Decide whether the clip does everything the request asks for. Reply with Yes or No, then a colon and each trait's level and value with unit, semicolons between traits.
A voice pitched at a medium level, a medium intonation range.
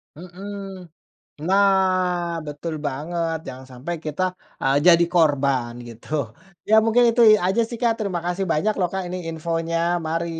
Yes: medium, 170 Hz; average, 3.8 semitones